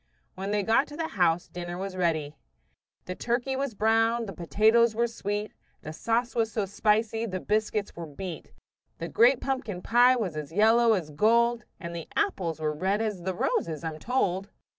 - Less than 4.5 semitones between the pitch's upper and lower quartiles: No, average, 4.9 semitones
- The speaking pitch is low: No, high, 210 Hz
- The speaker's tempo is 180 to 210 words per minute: Yes, average, 185 wpm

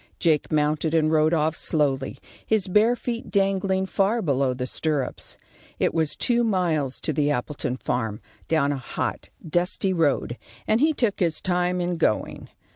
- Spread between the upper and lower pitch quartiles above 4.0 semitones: Yes, average, 4.8 semitones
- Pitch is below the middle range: No, medium, 160 Hz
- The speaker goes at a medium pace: Yes, average, 160 wpm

